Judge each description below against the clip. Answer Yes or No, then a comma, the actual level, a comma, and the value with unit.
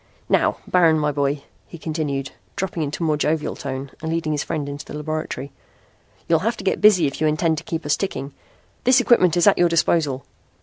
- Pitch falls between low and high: Yes, medium, 155 Hz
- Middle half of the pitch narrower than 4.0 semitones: Yes, average, 2.7 semitones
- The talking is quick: Yes, fast, 210 wpm